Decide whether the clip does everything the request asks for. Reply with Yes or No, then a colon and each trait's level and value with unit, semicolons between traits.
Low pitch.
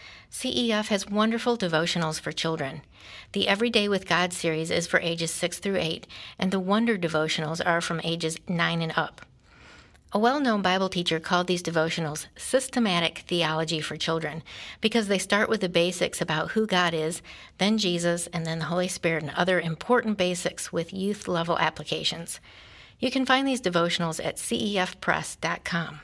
No: medium, 175 Hz